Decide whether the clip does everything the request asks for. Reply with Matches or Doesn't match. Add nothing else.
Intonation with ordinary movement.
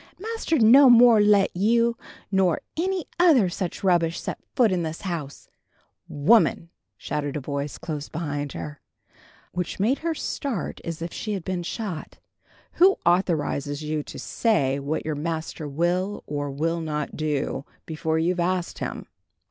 Doesn't match